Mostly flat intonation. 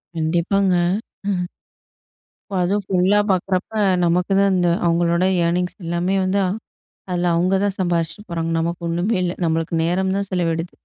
Yes: narrow, 2.0 semitones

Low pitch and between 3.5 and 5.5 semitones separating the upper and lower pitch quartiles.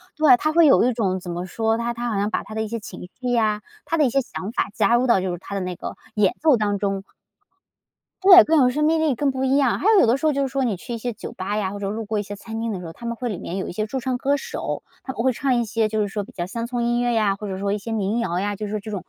No: high, 225 Hz; average, 3.9 semitones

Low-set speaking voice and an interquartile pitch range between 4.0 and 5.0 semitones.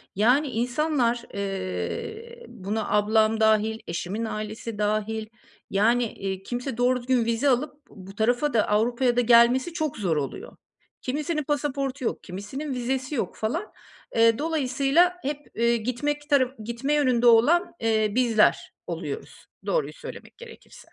No: high, 240 Hz; average, 4.7 semitones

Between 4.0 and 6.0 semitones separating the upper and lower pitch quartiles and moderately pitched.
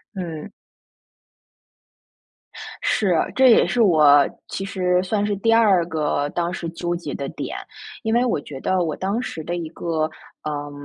Yes: average, 4.3 semitones; medium, 175 Hz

